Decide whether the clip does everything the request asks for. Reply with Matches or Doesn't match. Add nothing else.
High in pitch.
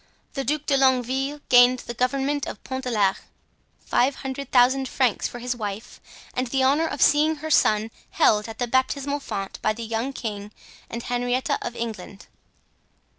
Matches